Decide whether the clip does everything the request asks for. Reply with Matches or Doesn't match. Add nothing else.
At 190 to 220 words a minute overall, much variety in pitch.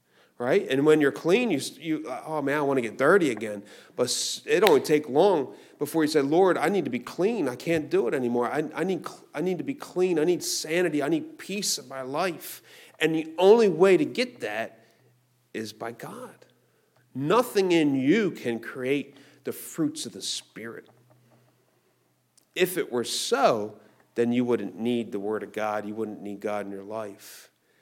Matches